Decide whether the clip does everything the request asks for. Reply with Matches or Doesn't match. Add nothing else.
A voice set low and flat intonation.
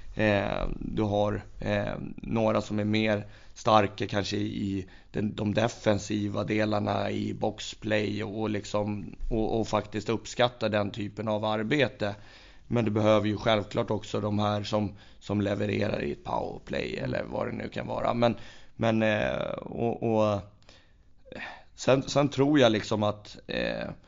Matches